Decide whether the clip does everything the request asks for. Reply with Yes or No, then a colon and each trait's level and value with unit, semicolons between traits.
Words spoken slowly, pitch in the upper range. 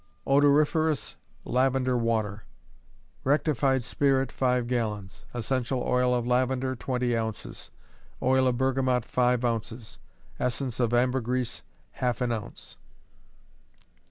No: slow, 100 wpm; low, 125 Hz